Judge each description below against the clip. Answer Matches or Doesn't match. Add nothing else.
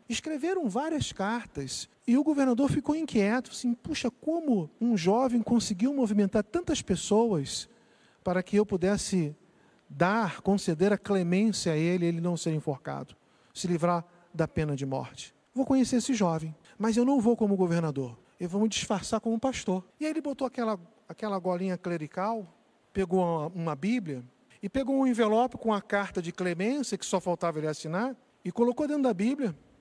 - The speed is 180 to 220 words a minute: Doesn't match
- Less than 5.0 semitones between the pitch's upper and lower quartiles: Doesn't match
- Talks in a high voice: Matches